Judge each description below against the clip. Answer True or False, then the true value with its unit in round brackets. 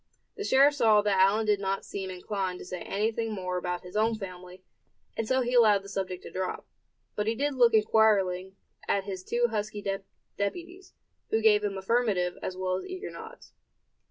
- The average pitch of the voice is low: False (205 Hz)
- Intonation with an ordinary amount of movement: True (3.2 semitones)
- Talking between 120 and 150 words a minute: False (185 wpm)